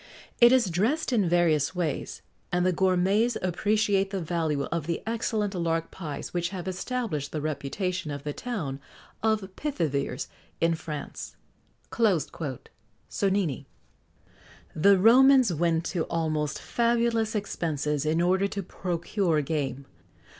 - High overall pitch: No, medium, 175 Hz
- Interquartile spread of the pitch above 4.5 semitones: Yes, average, 4.9 semitones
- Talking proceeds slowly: Yes, slow, 125 wpm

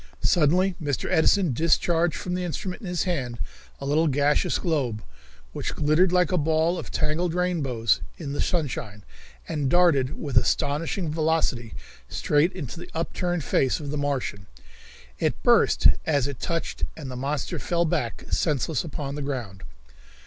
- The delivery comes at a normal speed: Yes, average, 155 wpm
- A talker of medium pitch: Yes, medium, 150 Hz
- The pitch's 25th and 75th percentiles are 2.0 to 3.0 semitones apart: No, average, 3.8 semitones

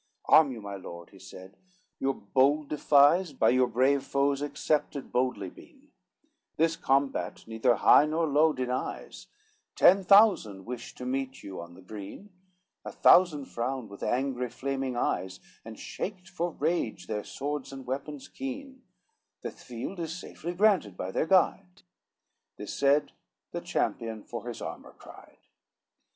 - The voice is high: No, low, 135 Hz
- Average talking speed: Yes, average, 150 wpm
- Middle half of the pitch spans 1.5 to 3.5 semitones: No, average, 5.3 semitones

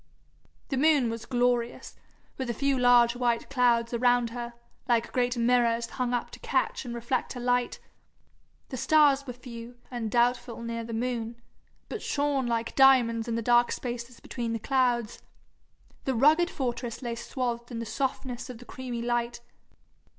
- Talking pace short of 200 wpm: Yes, average, 165 wpm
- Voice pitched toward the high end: Yes, high, 240 Hz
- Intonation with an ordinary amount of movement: No, narrow, 1.3 semitones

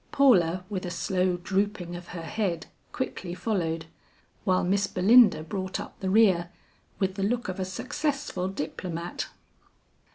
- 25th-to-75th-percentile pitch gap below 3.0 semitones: Yes, narrow, 2.6 semitones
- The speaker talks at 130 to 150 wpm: Yes, average, 140 wpm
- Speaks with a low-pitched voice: No, medium, 185 Hz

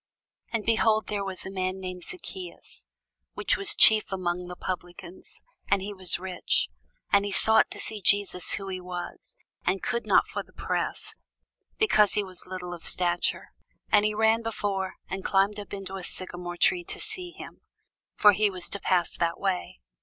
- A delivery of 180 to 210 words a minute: Yes, average, 185 wpm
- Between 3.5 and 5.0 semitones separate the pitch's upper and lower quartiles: No, narrow, 2.6 semitones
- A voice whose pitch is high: Yes, high, 195 Hz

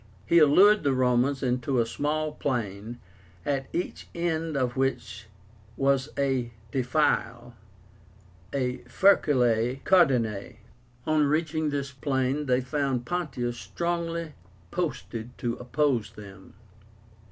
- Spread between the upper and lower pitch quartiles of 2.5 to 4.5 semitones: Yes, average, 4.0 semitones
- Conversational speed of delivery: No, slow, 105 wpm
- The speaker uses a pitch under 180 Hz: Yes, low, 135 Hz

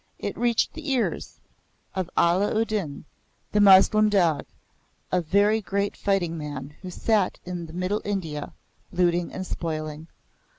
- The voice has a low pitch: No, medium, 185 Hz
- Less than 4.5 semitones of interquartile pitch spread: Yes, average, 3.8 semitones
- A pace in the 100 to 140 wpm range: Yes, slow, 135 wpm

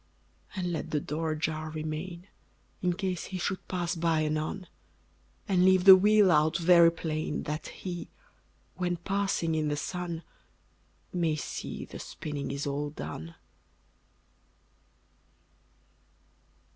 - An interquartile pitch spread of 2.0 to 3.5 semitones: Yes, average, 2.8 semitones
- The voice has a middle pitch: Yes, medium, 165 Hz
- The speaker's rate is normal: No, slow, 120 wpm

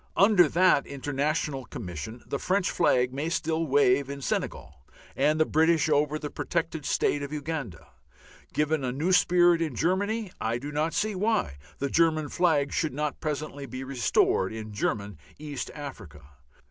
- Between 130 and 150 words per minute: No, average, 160 wpm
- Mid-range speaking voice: Yes, medium, 150 Hz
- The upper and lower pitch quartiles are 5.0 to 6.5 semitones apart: No, average, 3.9 semitones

